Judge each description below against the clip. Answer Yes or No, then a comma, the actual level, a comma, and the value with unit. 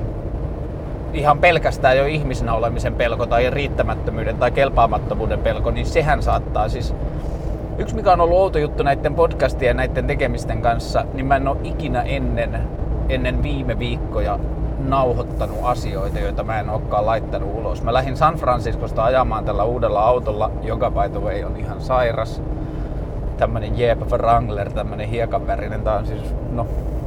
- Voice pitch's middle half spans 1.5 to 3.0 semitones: No, average, 3.8 semitones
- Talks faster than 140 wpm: Yes, average, 150 wpm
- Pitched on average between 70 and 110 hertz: No, low, 120 Hz